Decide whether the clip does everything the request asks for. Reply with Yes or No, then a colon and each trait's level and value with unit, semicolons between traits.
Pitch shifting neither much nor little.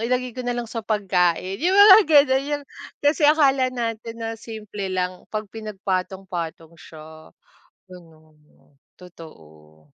No: wide, 6.8 semitones